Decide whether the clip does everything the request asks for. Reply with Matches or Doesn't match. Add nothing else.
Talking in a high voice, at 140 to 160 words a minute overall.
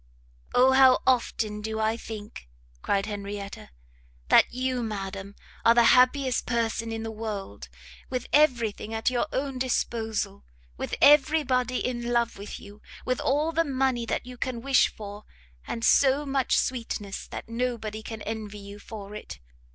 Matches